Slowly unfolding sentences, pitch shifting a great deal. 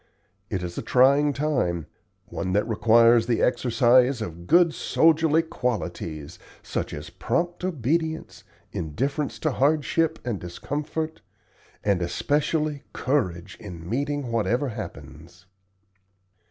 Yes: slow, 110 wpm; wide, 7.2 semitones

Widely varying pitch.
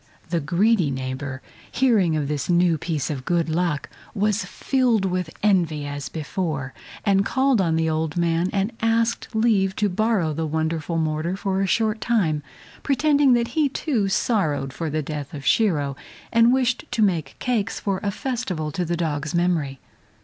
Yes: wide, 6.0 semitones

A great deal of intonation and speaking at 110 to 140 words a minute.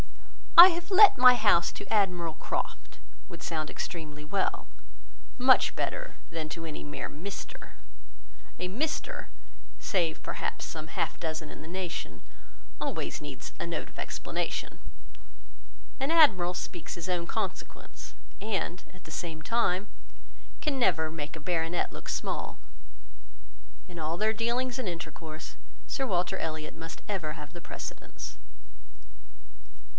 Yes: wide, 5.8 semitones; slow, 135 wpm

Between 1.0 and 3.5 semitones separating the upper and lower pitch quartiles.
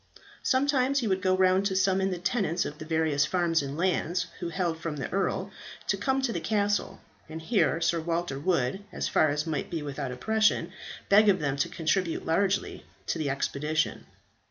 No: average, 3.9 semitones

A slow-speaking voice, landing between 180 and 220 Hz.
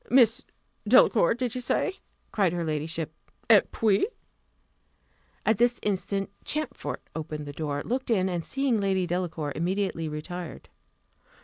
Yes: slow, 130 wpm; high, 190 Hz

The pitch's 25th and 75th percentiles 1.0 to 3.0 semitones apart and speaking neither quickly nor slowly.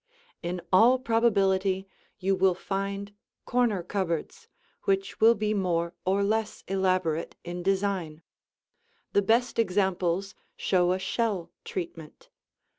No: average, 2.7 semitones; slow, 115 wpm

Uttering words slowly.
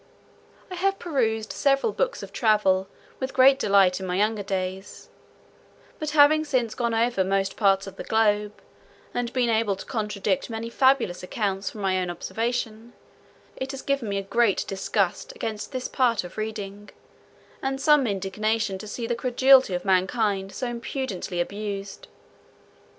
No: average, 155 wpm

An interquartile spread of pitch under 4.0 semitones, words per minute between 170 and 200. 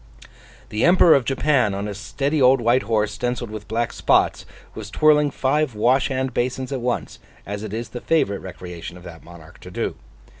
No: average, 4.3 semitones; average, 190 wpm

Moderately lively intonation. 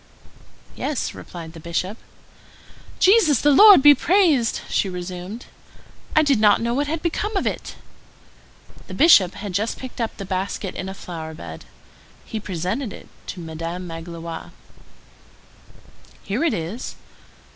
No: wide, 8.2 semitones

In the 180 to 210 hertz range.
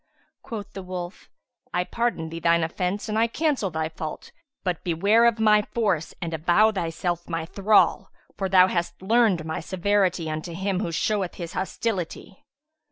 Yes: medium, 185 Hz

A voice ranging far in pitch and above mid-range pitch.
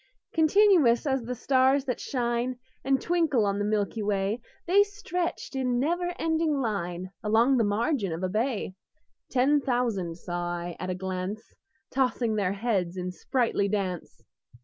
Yes: wide, 5.8 semitones; high, 235 Hz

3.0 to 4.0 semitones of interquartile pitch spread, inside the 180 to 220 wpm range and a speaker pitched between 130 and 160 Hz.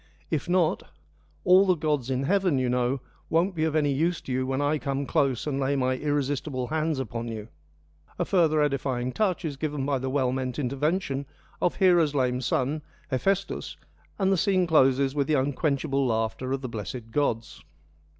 Yes: average, 3.5 semitones; average, 185 wpm; medium, 140 Hz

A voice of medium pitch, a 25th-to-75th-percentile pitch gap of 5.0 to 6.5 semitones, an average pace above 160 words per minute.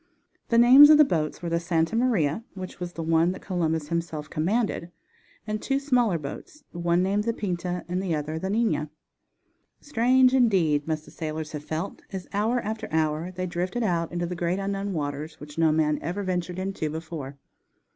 No: medium, 175 Hz; average, 4.4 semitones; average, 185 wpm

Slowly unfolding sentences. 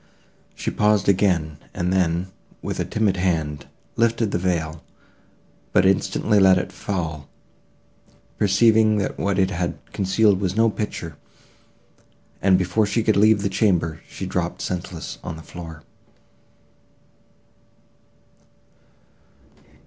Yes: slow, 115 wpm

